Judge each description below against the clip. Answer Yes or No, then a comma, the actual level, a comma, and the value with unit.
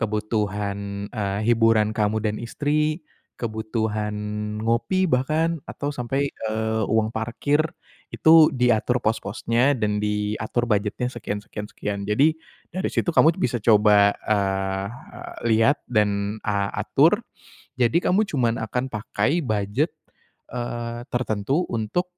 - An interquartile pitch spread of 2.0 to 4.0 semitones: Yes, average, 3.6 semitones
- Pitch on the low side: Yes, low, 110 Hz